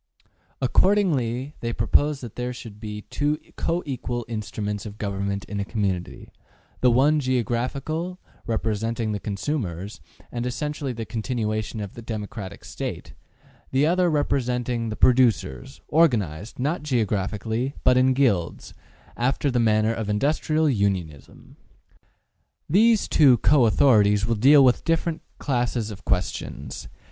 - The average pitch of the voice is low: Yes, low, 120 Hz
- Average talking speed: No, slow, 130 wpm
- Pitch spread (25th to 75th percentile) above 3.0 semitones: Yes, average, 4.8 semitones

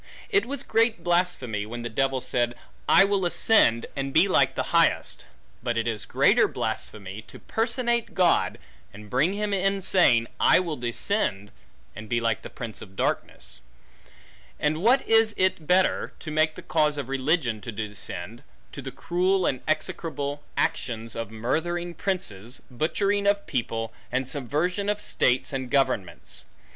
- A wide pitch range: Yes, wide, 8.2 semitones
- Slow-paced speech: No, average, 155 wpm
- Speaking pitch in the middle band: Yes, medium, 145 Hz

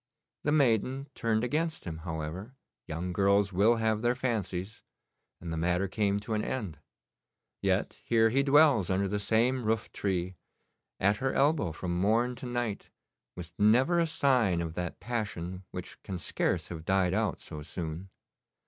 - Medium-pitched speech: No, low, 105 Hz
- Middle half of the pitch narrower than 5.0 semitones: No, average, 5.3 semitones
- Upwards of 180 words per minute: No, average, 160 wpm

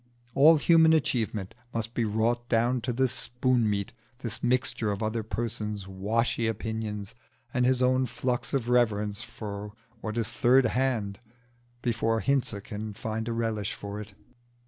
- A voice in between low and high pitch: No, low, 115 Hz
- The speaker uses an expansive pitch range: No, average, 2.7 semitones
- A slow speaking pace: No, average, 150 wpm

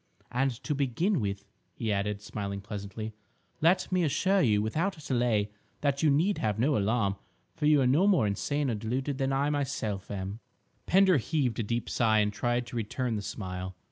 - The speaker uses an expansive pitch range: Yes, wide, 5.7 semitones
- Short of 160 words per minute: No, average, 185 wpm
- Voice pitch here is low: Yes, low, 120 Hz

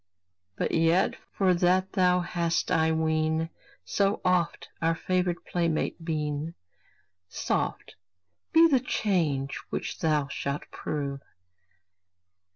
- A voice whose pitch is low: No, medium, 165 Hz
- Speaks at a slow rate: Yes, slow, 105 wpm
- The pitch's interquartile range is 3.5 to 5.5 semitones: No, narrow, 2.5 semitones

